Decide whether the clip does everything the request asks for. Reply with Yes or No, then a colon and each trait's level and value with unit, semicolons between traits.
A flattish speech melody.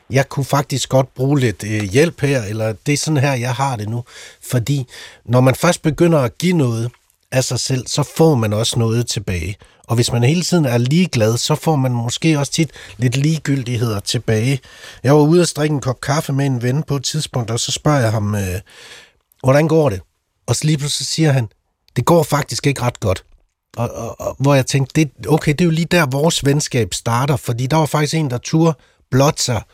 No: average, 4.3 semitones